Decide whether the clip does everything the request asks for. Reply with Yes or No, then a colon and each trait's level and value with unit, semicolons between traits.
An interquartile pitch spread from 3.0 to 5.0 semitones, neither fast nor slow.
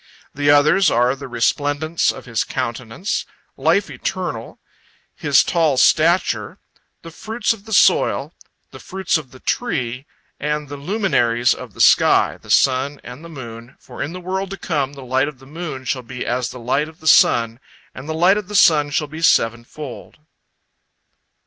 Yes: average, 4.7 semitones; average, 175 wpm